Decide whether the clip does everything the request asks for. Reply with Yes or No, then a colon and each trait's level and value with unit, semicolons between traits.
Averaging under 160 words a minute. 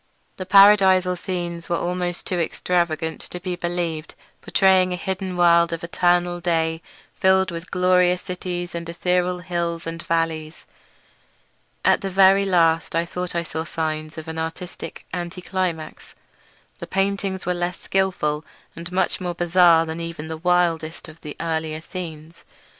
Yes: average, 150 wpm